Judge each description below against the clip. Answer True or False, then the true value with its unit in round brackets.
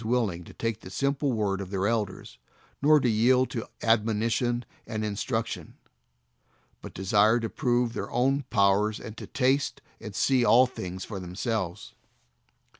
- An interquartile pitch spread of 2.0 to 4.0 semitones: True (3.4 semitones)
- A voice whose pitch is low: True (110 Hz)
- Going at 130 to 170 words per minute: True (160 wpm)